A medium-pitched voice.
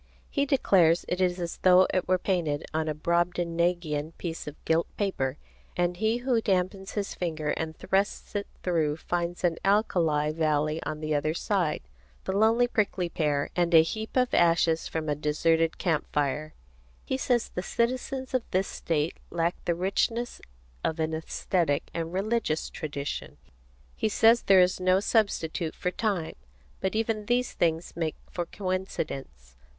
Yes: medium, 175 Hz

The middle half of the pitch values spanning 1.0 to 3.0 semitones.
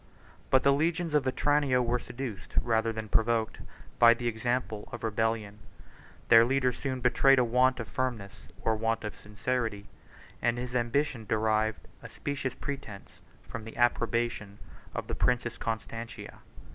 Yes: narrow, 2.5 semitones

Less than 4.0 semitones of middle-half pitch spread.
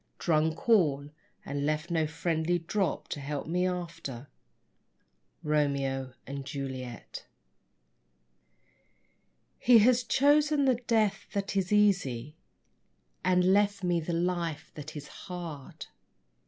No: wide, 5.4 semitones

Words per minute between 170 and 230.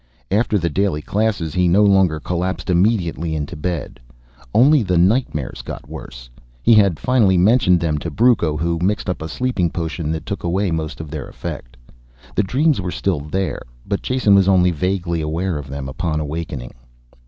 Yes: average, 175 wpm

